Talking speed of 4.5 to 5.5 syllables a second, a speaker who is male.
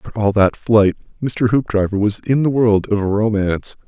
Yes: 4.7 syllables/s; male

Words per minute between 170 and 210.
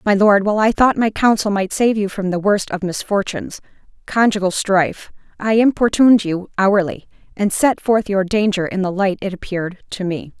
Yes: average, 190 wpm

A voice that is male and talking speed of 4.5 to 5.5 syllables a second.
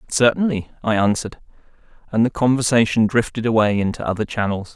No: male; 6.0 syllables/s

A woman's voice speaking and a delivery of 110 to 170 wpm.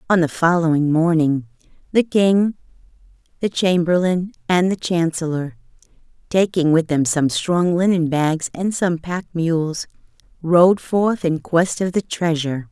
Yes: female; slow, 135 wpm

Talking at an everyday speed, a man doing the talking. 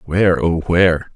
Yes: average, 155 wpm; male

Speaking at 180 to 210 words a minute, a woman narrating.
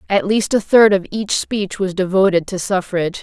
Yes: fast, 205 wpm; female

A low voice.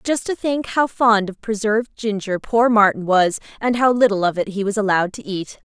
No: high, 215 Hz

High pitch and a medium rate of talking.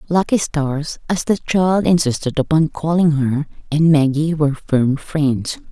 No: medium, 150 Hz; average, 145 wpm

